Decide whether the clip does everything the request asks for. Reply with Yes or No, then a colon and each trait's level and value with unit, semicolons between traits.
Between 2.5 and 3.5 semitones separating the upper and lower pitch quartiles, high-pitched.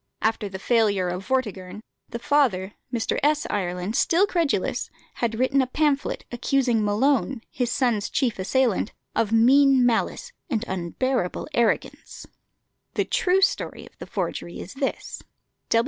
No: average, 4.8 semitones; high, 235 Hz